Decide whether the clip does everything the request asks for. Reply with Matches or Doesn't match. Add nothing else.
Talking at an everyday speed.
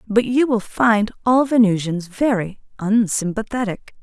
Doesn't match